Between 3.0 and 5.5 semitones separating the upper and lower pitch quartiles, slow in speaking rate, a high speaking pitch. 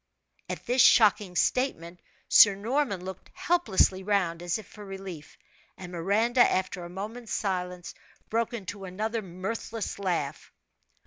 Yes: average, 3.7 semitones; slow, 130 wpm; high, 195 Hz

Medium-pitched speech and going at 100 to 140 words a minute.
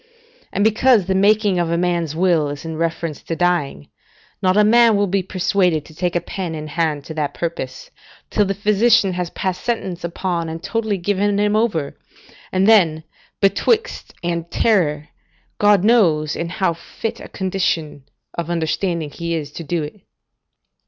No: medium, 175 Hz; average, 165 wpm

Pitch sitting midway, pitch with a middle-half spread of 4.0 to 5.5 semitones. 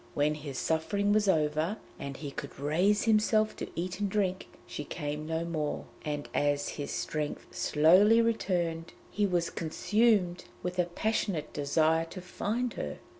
Yes: medium, 170 Hz; average, 5.2 semitones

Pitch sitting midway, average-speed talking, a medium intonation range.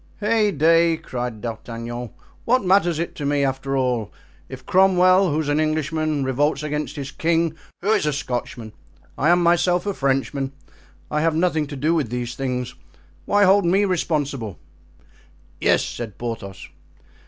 Yes: medium, 150 Hz; average, 145 wpm; average, 4.9 semitones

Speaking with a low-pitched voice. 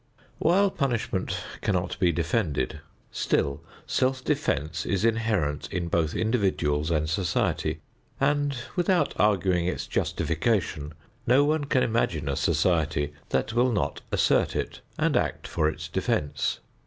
Yes: very low, 95 Hz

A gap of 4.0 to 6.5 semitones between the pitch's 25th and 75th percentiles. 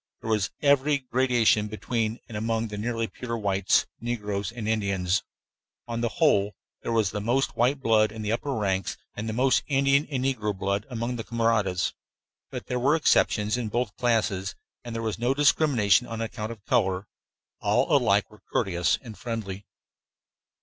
No: average, 3.0 semitones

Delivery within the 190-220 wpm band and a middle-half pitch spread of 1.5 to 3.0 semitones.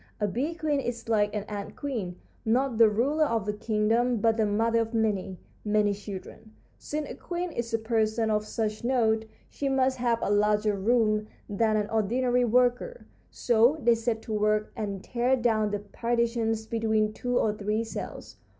No: average, 175 wpm; narrow, 2.4 semitones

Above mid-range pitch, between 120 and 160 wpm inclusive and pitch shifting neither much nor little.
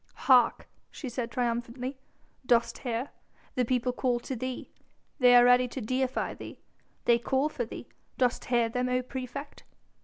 No: very high, 250 Hz; average, 155 wpm; narrow, 1.3 semitones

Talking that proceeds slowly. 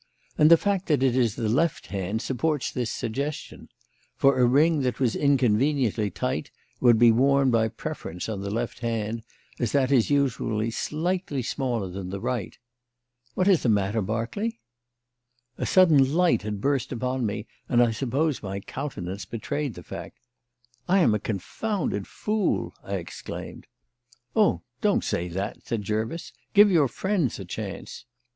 No: average, 160 wpm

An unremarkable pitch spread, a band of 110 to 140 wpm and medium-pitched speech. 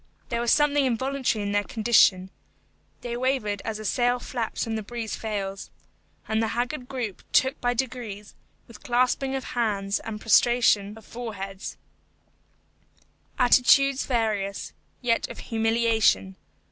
No: average, 3.0 semitones; slow, 135 wpm; high, 230 Hz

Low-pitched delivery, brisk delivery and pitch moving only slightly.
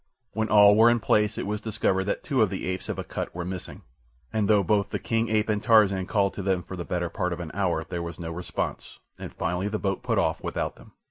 No: low, 100 Hz; fast, 255 wpm; average, 3.1 semitones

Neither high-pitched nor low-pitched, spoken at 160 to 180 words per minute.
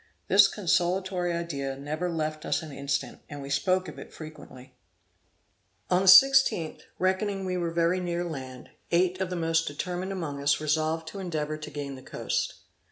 Yes: medium, 165 Hz; average, 170 wpm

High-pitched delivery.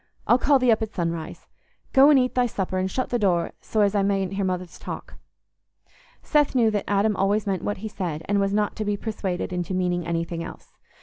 Yes: high, 200 Hz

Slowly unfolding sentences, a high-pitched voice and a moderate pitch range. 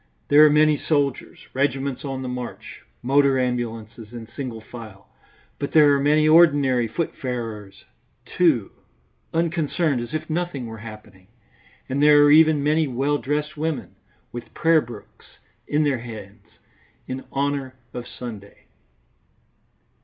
No: slow, 130 wpm; low, 135 Hz; average, 4.0 semitones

